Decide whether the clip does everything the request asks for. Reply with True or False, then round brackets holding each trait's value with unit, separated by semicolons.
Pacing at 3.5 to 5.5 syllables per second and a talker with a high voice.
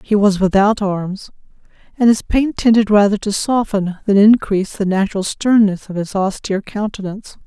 True (5.2 syllables/s; 205 Hz)